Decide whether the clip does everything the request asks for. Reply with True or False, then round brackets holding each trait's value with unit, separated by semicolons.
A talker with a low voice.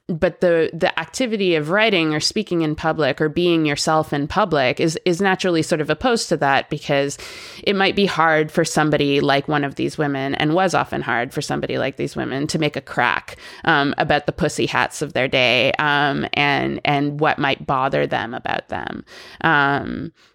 False (155 Hz)